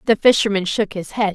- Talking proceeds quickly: Yes, fast, 225 wpm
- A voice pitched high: Yes, high, 205 Hz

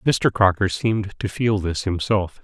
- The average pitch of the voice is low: Yes, low, 100 Hz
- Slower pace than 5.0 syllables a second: Yes, 4.5 syllables/s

